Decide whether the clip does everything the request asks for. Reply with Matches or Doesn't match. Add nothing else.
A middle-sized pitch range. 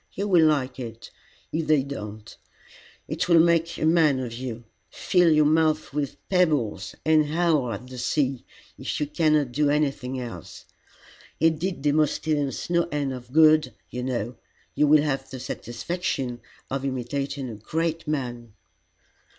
Matches